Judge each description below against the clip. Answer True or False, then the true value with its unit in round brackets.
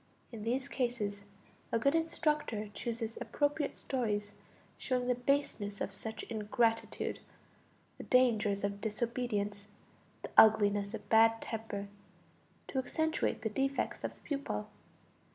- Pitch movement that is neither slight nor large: True (3.8 semitones)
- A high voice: True (225 Hz)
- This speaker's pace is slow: True (120 wpm)